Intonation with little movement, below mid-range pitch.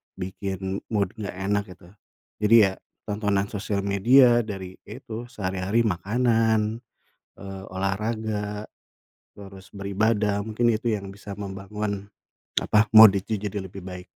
Yes: narrow, 2.0 semitones; low, 100 Hz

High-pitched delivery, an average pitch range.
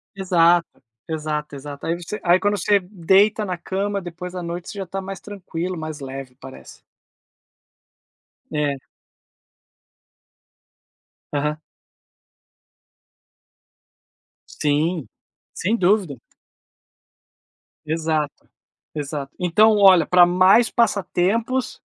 No: medium, 175 Hz; average, 4.2 semitones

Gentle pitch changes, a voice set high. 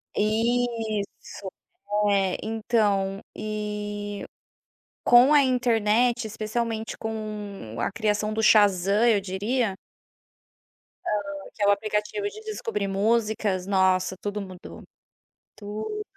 Yes: narrow, 2.3 semitones; high, 210 Hz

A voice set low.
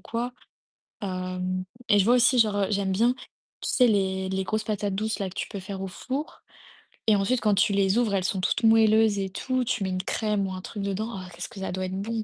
No: high, 200 Hz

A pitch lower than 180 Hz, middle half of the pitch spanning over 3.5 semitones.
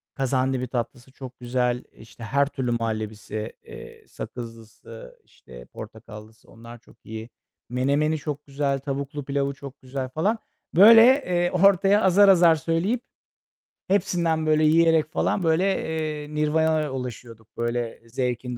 Yes: medium, 140 Hz; average, 4.9 semitones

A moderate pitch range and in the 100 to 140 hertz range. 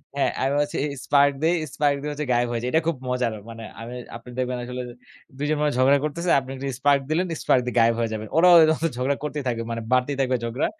Yes: average, 3.0 semitones; low, 135 Hz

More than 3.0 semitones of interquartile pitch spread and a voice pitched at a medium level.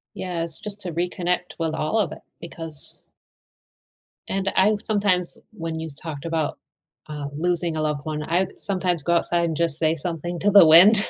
No: narrow, 2.5 semitones; medium, 170 Hz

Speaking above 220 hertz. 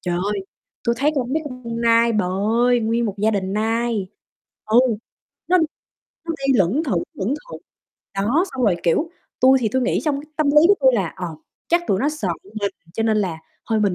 Yes: high, 230 Hz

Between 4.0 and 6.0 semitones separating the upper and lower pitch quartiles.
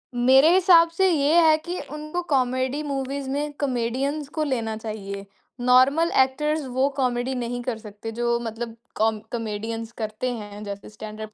Yes: average, 4.4 semitones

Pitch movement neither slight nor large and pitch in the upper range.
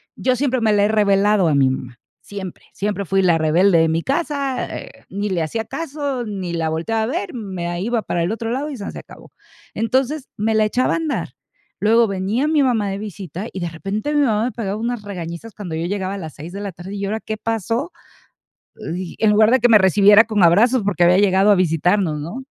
Yes: average, 4.3 semitones; high, 205 Hz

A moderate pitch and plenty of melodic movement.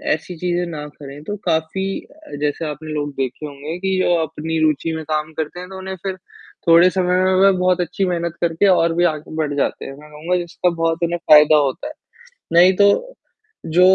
No: medium, 165 Hz; average, 2.9 semitones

